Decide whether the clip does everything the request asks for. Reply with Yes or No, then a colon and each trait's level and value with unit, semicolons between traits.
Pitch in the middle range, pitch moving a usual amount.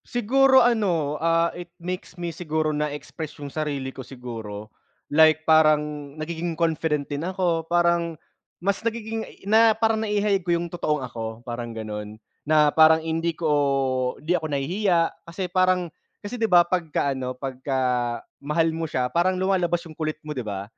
Yes: medium, 160 Hz; average, 3.9 semitones